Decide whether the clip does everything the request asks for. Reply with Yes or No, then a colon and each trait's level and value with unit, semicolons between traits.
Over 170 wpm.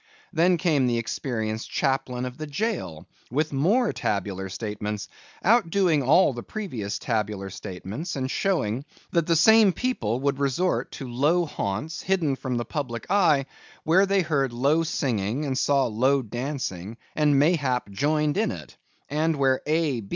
No: average, 150 wpm